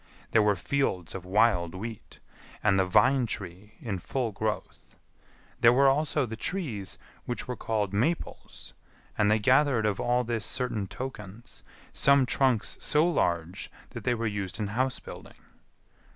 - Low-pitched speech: Yes, low, 110 Hz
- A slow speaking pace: No, average, 150 wpm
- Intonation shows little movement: No, average, 4.3 semitones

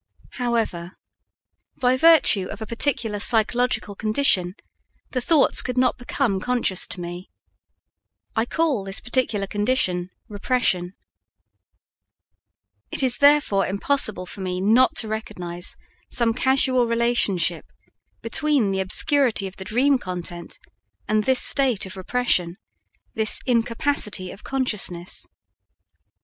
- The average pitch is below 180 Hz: No, high, 220 Hz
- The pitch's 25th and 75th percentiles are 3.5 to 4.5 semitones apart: No, average, 5.0 semitones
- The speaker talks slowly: Yes, slow, 115 wpm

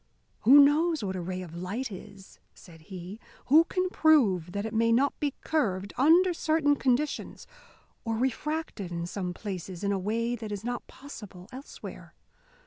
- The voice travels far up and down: Yes, wide, 7.4 semitones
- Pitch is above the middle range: Yes, high, 225 Hz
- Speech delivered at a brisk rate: No, average, 165 wpm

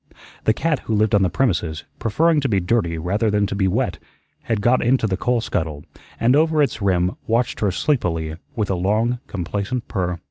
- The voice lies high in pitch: No, low, 105 Hz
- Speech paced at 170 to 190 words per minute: No, average, 200 wpm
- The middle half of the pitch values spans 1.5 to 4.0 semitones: No, average, 5.0 semitones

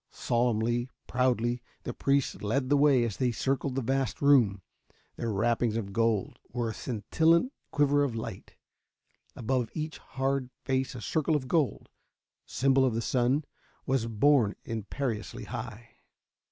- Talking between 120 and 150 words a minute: Yes, average, 140 wpm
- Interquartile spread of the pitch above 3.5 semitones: No, average, 3.2 semitones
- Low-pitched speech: Yes, low, 125 Hz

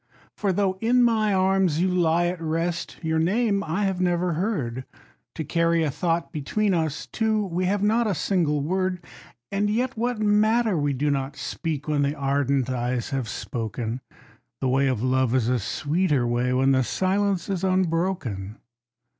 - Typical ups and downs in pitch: No, wide, 5.9 semitones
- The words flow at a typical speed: Yes, average, 170 wpm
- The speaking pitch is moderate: Yes, medium, 170 Hz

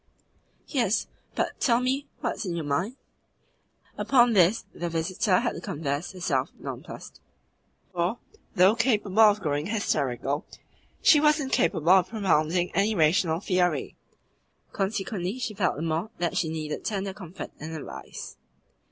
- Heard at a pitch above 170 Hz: Yes, medium, 185 Hz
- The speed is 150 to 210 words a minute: No, average, 140 wpm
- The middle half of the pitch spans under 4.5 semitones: No, average, 5.0 semitones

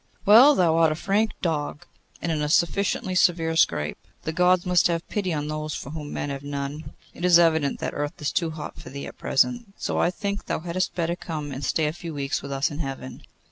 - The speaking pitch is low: No, medium, 160 Hz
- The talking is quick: Yes, fast, 230 wpm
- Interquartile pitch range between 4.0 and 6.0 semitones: No, average, 3.4 semitones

